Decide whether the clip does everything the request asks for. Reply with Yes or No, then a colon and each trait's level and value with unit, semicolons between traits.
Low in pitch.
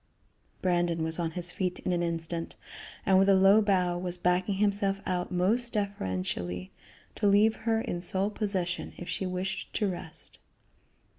No: medium, 180 Hz